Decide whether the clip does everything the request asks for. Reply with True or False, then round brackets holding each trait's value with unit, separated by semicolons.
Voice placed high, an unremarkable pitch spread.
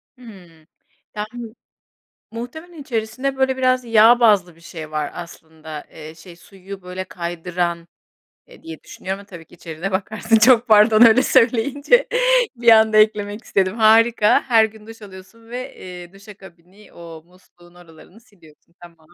True (205 Hz; 4.7 semitones)